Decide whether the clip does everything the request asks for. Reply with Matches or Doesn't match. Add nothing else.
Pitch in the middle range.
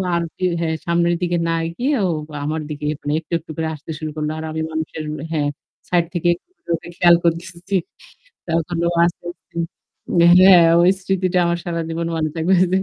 Matches